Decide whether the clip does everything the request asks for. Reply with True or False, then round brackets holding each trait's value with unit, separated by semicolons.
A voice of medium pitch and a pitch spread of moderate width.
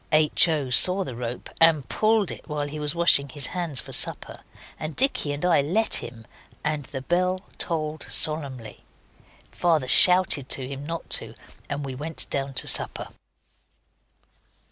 True (150 Hz; 3.6 semitones)